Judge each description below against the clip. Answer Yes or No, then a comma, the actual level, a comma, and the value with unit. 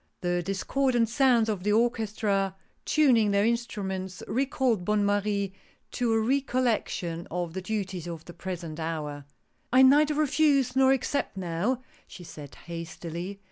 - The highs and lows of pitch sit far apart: Yes, wide, 5.9 semitones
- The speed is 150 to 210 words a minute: No, average, 140 wpm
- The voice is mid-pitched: No, high, 205 Hz